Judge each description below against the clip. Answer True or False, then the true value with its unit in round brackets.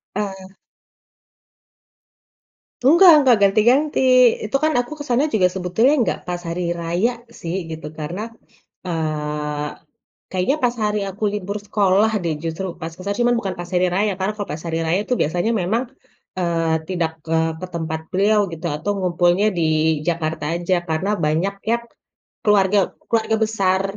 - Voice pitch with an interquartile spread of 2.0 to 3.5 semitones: False (4.2 semitones)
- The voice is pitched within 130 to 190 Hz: True (185 Hz)